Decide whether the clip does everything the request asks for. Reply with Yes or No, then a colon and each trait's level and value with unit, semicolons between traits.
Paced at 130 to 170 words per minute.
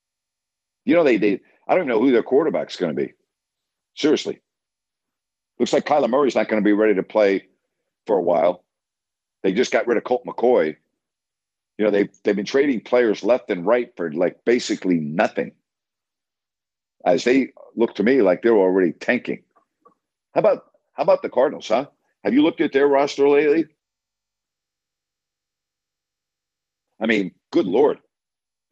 Yes: average, 160 wpm